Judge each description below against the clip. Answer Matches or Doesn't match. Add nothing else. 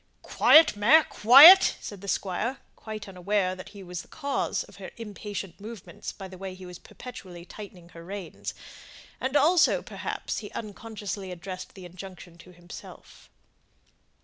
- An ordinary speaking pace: Matches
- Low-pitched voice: Doesn't match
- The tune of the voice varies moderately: Matches